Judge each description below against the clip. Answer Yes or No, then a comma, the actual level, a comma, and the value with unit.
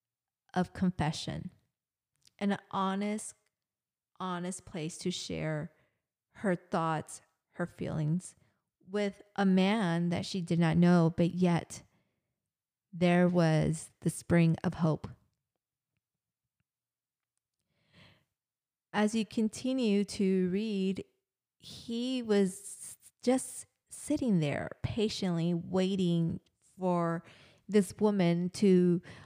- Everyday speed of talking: No, slow, 90 wpm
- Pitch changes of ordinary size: Yes, average, 3.5 semitones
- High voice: No, medium, 180 Hz